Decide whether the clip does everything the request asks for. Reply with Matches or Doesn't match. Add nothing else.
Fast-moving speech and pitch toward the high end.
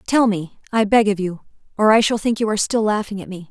Matches